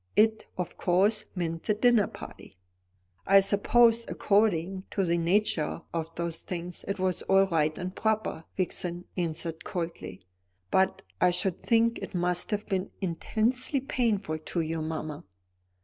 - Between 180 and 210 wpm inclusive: No, average, 145 wpm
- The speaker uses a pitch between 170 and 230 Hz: Yes, medium, 185 Hz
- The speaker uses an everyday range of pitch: Yes, average, 3.9 semitones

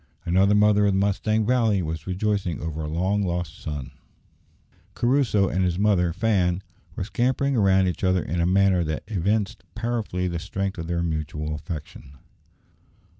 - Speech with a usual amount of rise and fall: Yes, average, 3.5 semitones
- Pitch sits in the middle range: No, very low, 95 Hz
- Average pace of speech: Yes, average, 160 wpm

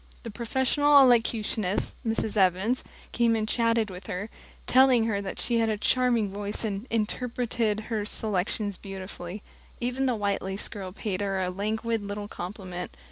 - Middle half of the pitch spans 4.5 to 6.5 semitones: No, average, 2.8 semitones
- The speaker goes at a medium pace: Yes, average, 155 wpm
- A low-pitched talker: No, high, 215 Hz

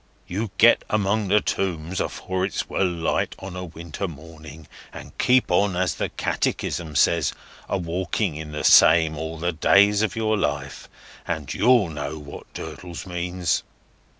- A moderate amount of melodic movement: Yes, average, 3.7 semitones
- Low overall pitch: Yes, very low, 90 Hz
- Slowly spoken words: No, average, 155 wpm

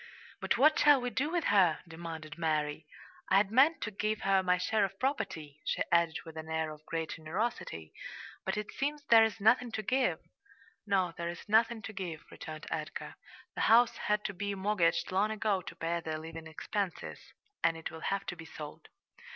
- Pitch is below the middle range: No, high, 190 Hz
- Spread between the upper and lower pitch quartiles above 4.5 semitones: Yes, average, 5.2 semitones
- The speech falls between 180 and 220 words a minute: Yes, average, 190 wpm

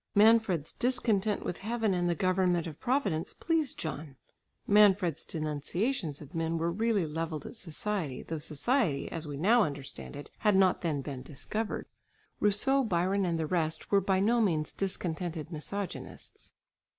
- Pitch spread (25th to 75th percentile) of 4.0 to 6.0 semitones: Yes, average, 4.9 semitones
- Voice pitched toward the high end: No, medium, 180 Hz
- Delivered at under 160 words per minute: Yes, average, 150 wpm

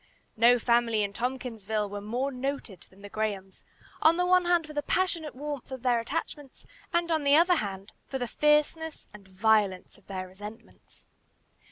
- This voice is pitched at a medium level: No, high, 245 Hz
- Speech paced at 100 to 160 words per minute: No, average, 170 wpm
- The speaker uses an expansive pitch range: Yes, wide, 6.1 semitones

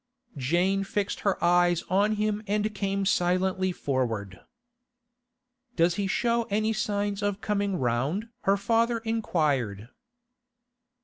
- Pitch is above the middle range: Yes, high, 195 Hz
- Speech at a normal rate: No, slow, 115 wpm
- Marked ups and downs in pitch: No, average, 3.4 semitones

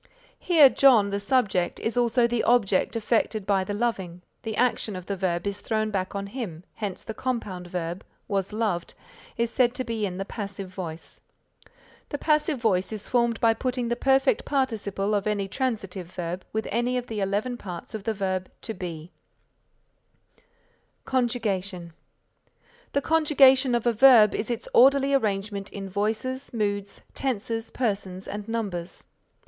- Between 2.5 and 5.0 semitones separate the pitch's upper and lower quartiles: Yes, average, 3.9 semitones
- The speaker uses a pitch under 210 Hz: No, high, 215 Hz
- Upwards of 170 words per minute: No, average, 160 wpm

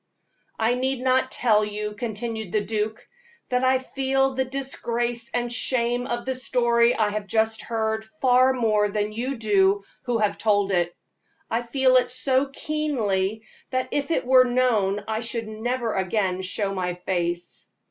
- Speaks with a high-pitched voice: Yes, high, 230 Hz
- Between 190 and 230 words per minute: No, average, 160 wpm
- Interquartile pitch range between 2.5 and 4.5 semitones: Yes, average, 3.4 semitones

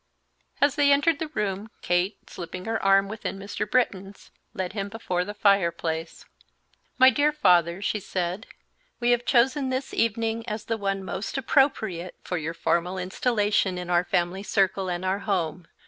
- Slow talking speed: No, average, 160 wpm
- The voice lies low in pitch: No, high, 195 Hz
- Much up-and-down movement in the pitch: No, average, 4.1 semitones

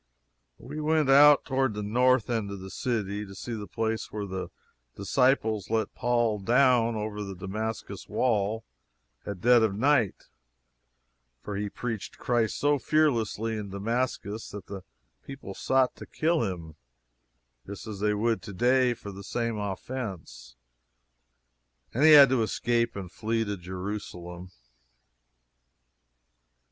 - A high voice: No, low, 110 Hz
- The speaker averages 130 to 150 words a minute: Yes, average, 140 wpm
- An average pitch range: Yes, average, 3.6 semitones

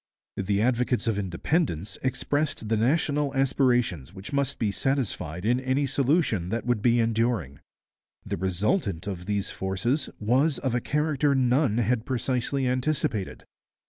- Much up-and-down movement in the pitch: No, average, 4.9 semitones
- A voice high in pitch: No, low, 120 Hz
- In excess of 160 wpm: No, average, 140 wpm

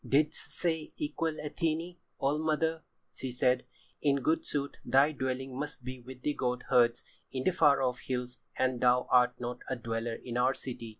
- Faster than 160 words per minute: Yes, average, 180 wpm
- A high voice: No, low, 130 Hz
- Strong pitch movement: No, average, 3.2 semitones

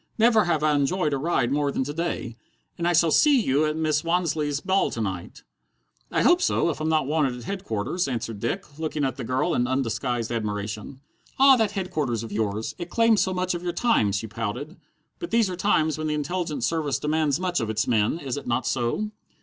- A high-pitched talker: No, medium, 150 Hz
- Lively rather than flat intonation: Yes, wide, 6.4 semitones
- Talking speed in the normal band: No, fast, 215 wpm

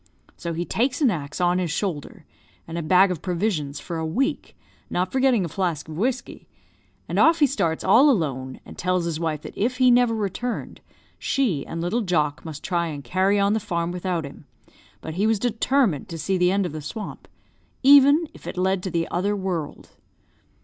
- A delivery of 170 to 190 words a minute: No, average, 200 wpm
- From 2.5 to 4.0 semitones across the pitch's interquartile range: No, average, 5.3 semitones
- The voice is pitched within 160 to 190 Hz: Yes, medium, 185 Hz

